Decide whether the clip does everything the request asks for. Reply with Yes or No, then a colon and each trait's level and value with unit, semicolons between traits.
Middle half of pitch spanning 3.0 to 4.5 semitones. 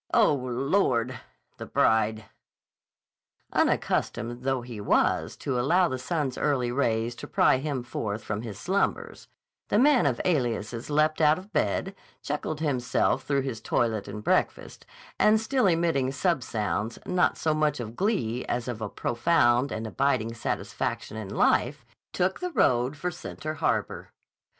No: average, 5.3 semitones